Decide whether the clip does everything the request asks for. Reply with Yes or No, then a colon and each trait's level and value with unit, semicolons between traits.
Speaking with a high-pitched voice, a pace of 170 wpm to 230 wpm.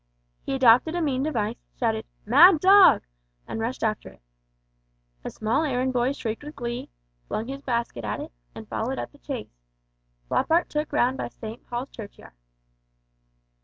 No: high, 245 Hz; average, 160 wpm